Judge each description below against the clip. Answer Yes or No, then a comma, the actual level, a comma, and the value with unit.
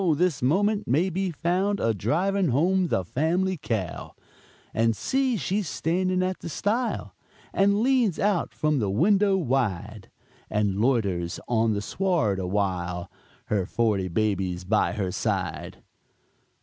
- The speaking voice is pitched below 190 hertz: Yes, medium, 140 Hz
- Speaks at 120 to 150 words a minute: Yes, slow, 135 wpm